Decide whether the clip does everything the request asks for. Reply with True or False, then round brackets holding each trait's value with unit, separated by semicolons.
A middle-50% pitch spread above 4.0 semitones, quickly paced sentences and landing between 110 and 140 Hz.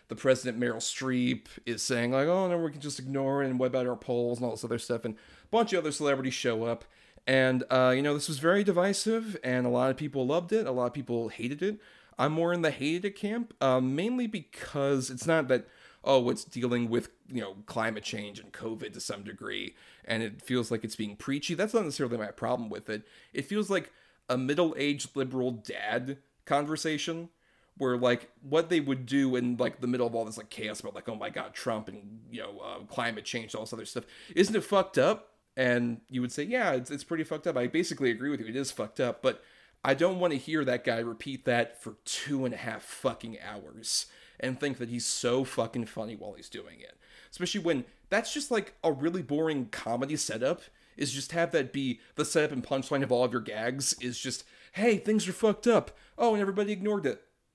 True (5.4 semitones; 230 wpm; 135 Hz)